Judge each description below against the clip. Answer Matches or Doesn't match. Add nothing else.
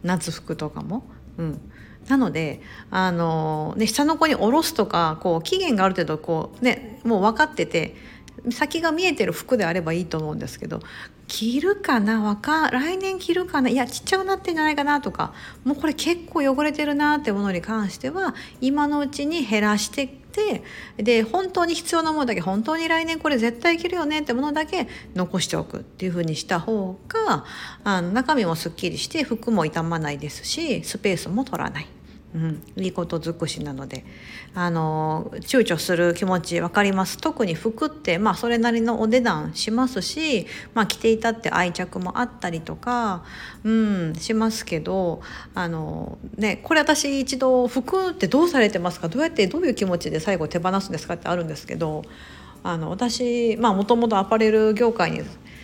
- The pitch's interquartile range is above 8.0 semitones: Matches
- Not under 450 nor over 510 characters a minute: Doesn't match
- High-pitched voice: Matches